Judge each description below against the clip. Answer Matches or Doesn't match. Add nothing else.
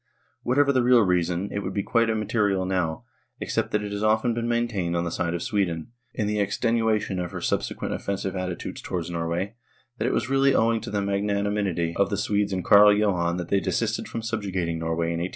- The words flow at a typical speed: Doesn't match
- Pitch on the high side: Doesn't match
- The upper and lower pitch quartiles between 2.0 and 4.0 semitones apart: Matches